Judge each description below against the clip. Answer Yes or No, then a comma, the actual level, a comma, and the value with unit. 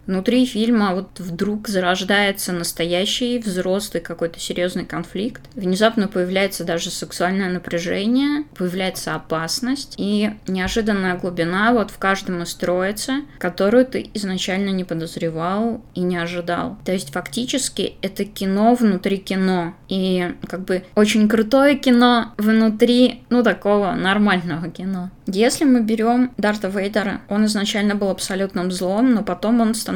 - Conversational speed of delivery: Yes, average, 130 wpm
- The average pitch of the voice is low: No, high, 195 Hz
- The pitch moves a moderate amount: Yes, average, 3.5 semitones